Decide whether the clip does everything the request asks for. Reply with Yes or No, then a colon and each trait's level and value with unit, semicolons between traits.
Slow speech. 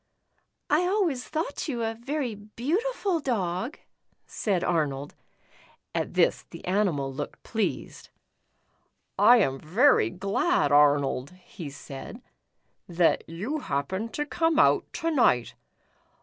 Yes: slow, 120 wpm